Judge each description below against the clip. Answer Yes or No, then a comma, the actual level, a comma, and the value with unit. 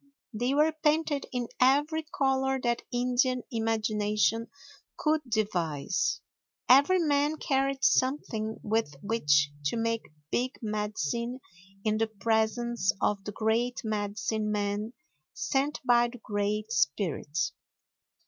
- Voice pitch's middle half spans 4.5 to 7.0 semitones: No, average, 4.0 semitones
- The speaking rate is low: Yes, slow, 110 wpm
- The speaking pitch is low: No, high, 230 Hz